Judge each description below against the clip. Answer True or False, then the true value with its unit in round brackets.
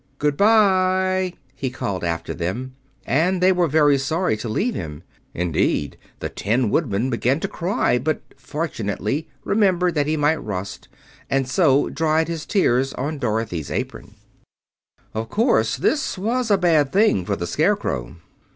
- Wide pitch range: True (8.3 semitones)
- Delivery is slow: False (150 wpm)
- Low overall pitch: False (145 Hz)